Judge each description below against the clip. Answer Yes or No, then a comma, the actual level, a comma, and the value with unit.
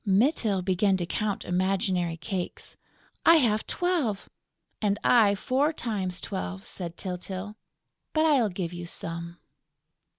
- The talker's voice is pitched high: Yes, high, 195 Hz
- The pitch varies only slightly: No, average, 3.9 semitones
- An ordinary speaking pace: No, slow, 125 wpm